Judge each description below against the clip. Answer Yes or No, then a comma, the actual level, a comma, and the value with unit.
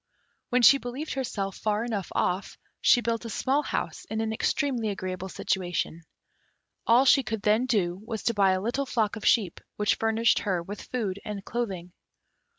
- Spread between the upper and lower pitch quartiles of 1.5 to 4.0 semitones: Yes, average, 3.6 semitones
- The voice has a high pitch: Yes, high, 220 Hz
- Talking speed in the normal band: Yes, average, 175 wpm